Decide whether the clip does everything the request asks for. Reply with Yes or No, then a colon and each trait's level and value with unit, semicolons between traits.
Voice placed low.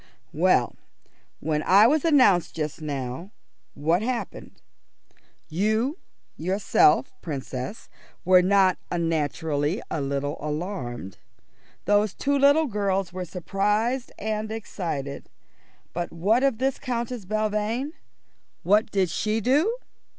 No: high, 195 Hz